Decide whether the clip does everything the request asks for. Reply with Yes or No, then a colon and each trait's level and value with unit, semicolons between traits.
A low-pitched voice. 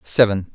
Yes: low, 105 Hz